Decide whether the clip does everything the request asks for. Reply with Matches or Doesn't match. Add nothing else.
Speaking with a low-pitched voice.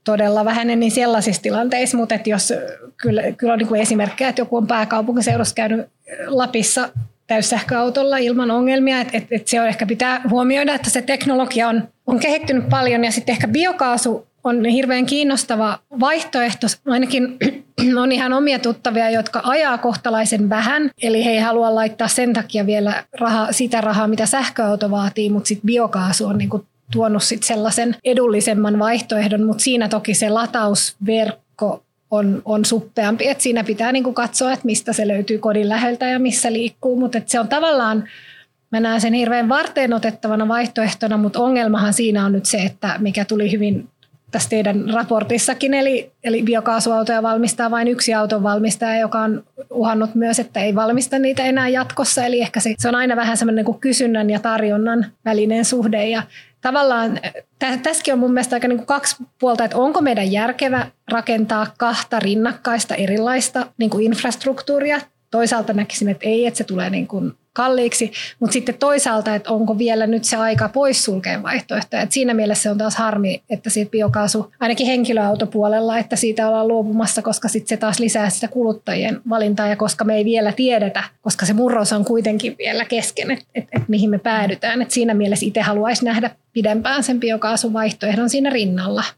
Doesn't match